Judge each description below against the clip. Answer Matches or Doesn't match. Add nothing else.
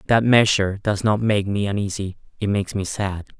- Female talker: Doesn't match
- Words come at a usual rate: Matches